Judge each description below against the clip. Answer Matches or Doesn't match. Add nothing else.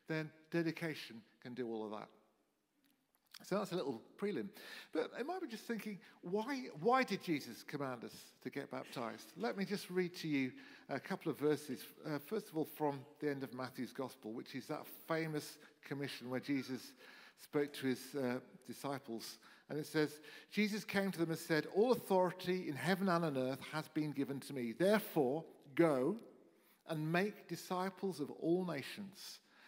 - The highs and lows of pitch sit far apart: Matches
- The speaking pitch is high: Doesn't match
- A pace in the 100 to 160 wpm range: Doesn't match